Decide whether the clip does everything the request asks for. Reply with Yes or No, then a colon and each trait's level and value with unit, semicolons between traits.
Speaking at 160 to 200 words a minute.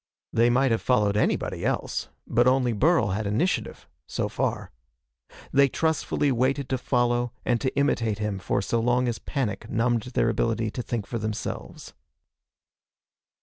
No: average, 150 wpm